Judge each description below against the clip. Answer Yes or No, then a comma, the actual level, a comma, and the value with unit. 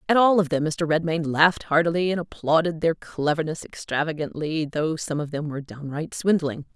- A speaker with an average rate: Yes, average, 180 wpm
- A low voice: No, medium, 160 Hz